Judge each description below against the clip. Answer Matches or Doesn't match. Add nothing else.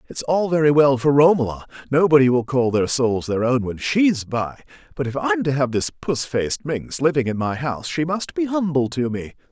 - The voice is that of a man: Matches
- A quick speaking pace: Matches